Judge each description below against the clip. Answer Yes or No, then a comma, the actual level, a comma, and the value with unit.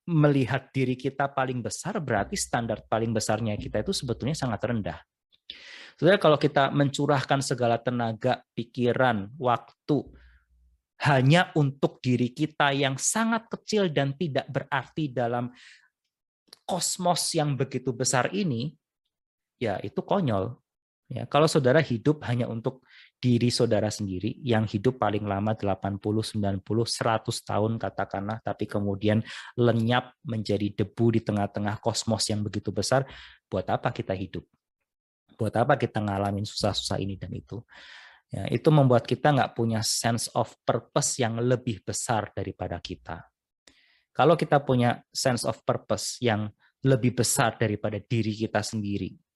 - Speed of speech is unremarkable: Yes, average, 130 wpm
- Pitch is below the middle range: Yes, low, 120 Hz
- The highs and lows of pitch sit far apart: No, average, 4.3 semitones